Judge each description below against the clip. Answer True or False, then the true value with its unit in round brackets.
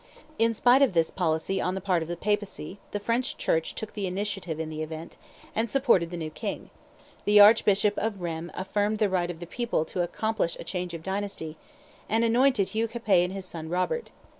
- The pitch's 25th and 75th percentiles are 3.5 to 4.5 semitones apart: True (4.1 semitones)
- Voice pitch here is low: False (195 Hz)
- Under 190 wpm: False (205 wpm)